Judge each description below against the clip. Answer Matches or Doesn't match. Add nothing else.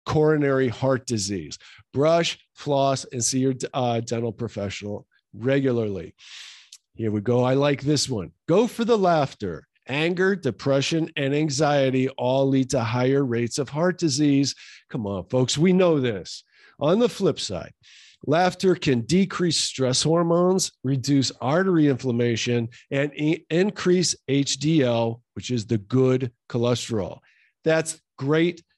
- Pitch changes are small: Doesn't match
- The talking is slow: Matches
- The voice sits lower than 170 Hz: Matches